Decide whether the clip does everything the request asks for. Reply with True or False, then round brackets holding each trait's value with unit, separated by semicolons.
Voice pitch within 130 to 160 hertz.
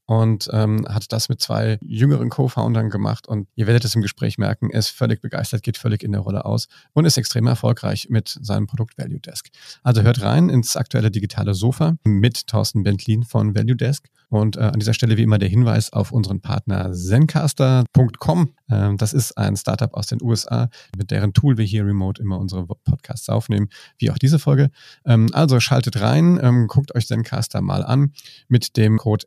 False (115 Hz)